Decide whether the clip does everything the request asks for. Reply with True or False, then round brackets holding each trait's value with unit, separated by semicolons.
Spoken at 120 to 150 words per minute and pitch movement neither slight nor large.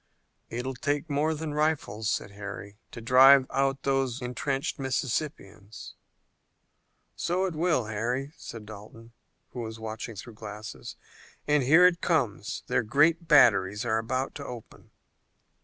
True (140 wpm; 4.8 semitones)